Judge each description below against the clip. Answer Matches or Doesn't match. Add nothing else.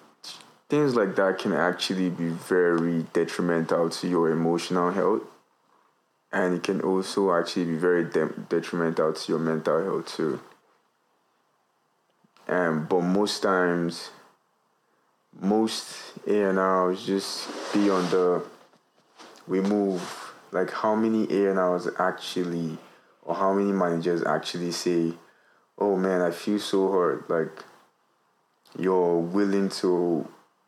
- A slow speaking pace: Matches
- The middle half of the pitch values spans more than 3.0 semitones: Doesn't match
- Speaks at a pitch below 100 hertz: Matches